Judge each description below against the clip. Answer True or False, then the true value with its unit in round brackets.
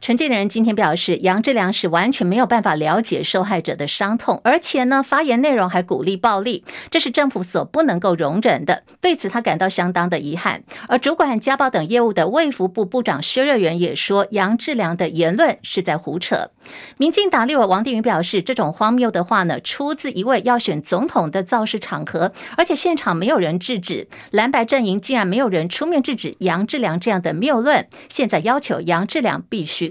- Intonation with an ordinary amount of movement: False (6.3 semitones)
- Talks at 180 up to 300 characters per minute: False (315 characters per minute)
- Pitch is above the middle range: True (225 Hz)